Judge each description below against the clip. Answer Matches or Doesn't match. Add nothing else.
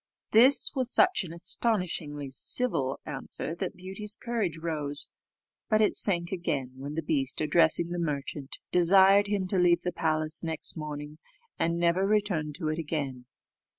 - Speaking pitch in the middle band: Matches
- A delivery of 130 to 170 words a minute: Matches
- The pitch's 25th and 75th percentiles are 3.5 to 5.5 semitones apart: Matches